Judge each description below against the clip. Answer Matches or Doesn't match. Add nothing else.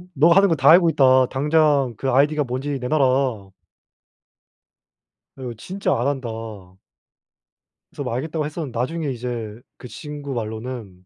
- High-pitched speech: Doesn't match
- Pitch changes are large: Doesn't match